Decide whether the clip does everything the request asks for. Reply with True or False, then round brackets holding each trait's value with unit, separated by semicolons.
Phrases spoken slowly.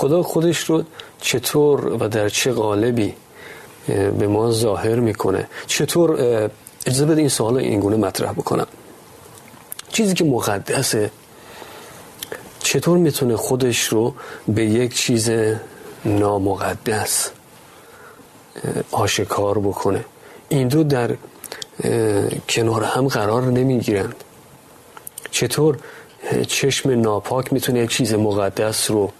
True (100 wpm)